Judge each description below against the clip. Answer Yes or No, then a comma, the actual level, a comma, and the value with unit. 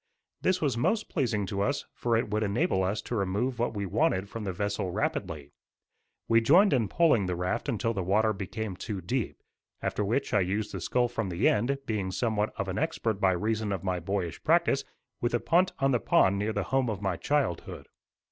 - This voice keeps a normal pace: No, fast, 210 wpm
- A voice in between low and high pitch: No, low, 105 Hz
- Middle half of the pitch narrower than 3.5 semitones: No, average, 3.8 semitones